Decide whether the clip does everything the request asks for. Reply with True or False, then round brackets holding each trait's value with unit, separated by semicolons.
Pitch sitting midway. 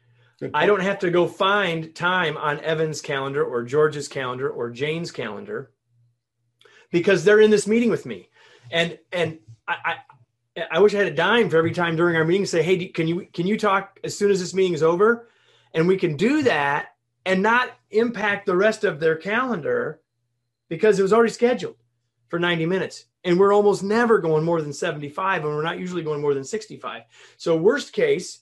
True (170 Hz)